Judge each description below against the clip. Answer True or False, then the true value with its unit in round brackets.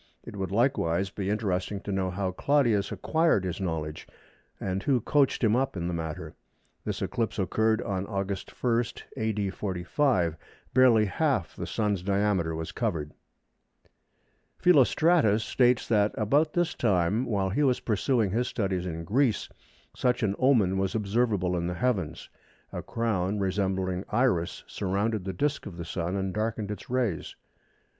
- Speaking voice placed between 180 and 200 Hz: False (100 Hz)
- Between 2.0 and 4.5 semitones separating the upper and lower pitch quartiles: True (4.2 semitones)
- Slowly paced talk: False (150 wpm)